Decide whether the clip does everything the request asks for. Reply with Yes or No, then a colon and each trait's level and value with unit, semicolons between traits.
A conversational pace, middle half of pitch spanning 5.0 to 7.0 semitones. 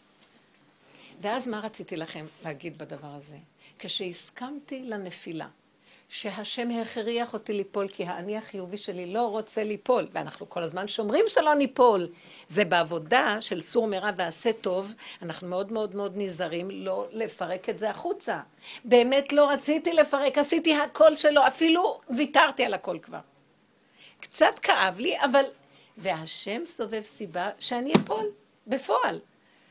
Yes: average, 130 wpm; wide, 5.4 semitones